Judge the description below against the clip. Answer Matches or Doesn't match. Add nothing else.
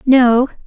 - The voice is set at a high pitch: Matches